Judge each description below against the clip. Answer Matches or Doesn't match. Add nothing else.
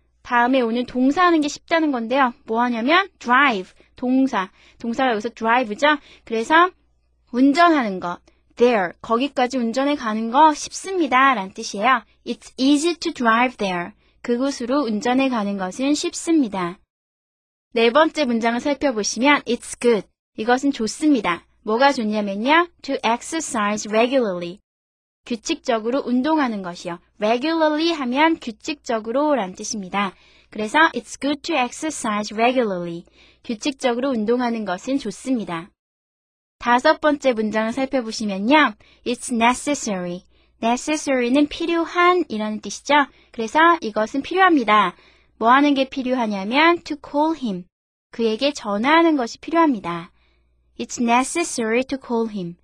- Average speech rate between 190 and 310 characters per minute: Doesn't match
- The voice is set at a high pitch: Matches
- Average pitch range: Matches